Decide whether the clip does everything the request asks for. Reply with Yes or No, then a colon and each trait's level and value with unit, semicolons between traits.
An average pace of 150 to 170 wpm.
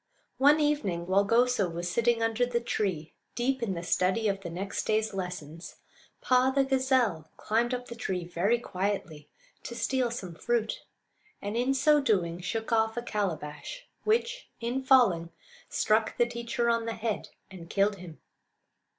Yes: average, 160 wpm